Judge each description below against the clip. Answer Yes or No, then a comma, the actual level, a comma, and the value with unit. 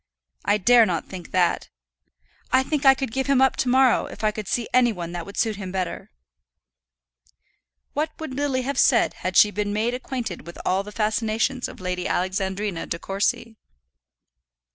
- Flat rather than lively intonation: No, average, 5.3 semitones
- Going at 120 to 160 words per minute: No, average, 180 wpm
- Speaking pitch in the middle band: No, high, 215 Hz